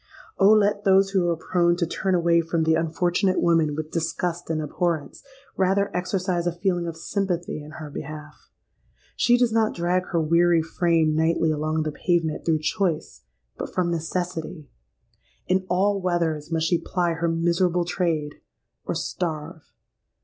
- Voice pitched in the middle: Yes, medium, 170 Hz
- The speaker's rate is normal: Yes, average, 155 wpm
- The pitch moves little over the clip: Yes, narrow, 2.3 semitones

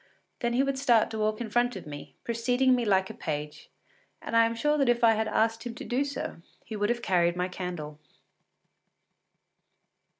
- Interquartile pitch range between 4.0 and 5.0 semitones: Yes, average, 4.3 semitones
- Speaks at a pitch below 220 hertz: No, high, 225 Hz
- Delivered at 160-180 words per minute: No, average, 200 wpm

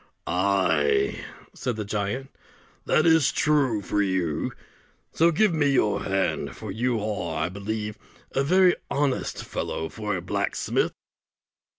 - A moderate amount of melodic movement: No, wide, 6.5 semitones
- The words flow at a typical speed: No, slow, 130 wpm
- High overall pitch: No, low, 105 Hz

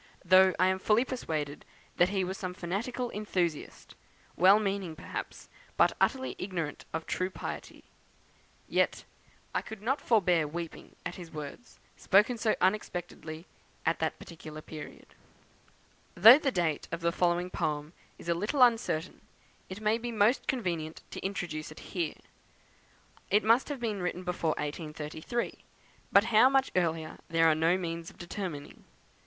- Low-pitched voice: No, medium, 180 Hz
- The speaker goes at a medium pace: Yes, average, 150 wpm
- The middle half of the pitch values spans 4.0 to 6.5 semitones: Yes, average, 4.6 semitones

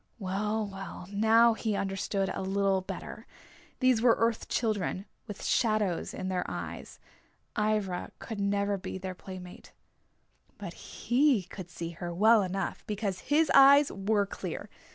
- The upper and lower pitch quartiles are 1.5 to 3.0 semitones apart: Yes, average, 2.7 semitones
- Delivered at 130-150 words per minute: Yes, average, 140 wpm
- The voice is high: Yes, high, 200 Hz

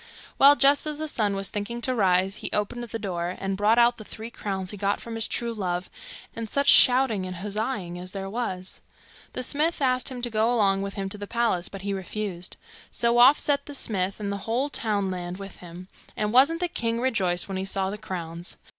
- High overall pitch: Yes, high, 210 Hz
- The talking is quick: Yes, fast, 220 wpm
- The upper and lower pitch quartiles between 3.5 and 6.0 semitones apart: Yes, average, 4.0 semitones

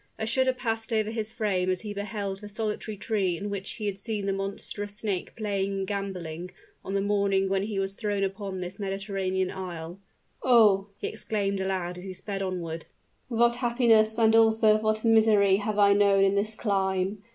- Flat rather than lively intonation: Yes, narrow, 2.0 semitones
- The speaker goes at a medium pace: Yes, average, 185 wpm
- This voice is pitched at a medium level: No, high, 200 Hz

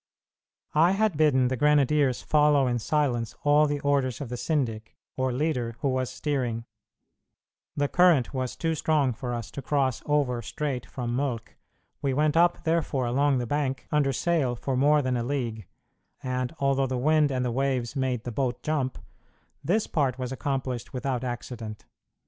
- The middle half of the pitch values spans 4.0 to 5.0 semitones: No, average, 3.1 semitones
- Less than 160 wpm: No, average, 170 wpm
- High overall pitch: No, low, 135 Hz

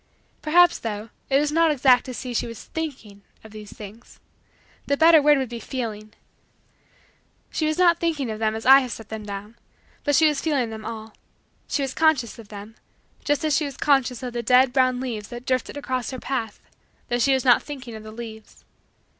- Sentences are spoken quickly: Yes, fast, 210 wpm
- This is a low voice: No, very high, 250 Hz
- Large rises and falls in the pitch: No, average, 4.5 semitones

